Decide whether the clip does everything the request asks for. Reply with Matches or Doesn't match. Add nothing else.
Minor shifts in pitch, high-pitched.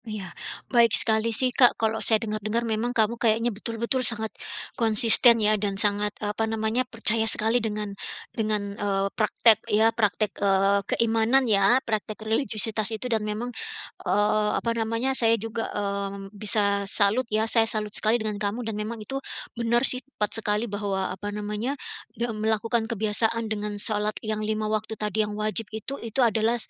Matches